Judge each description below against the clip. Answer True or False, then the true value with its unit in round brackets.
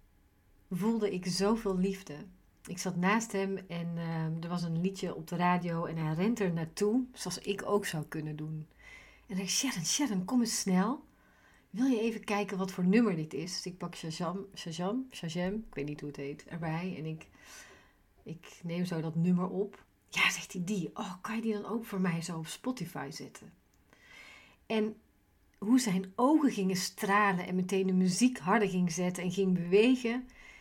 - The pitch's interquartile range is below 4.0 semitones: True (3.6 semitones)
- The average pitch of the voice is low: False (190 Hz)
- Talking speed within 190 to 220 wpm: True (195 wpm)